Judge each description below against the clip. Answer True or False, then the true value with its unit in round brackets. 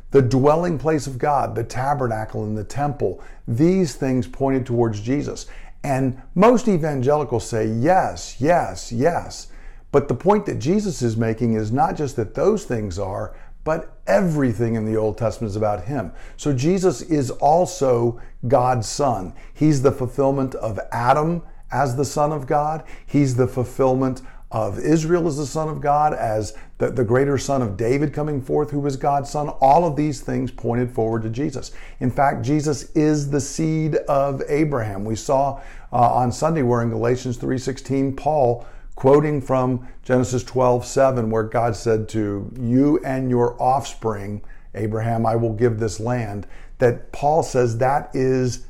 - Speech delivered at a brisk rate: False (165 wpm)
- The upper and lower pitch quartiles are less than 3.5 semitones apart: False (3.8 semitones)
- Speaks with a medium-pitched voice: False (130 Hz)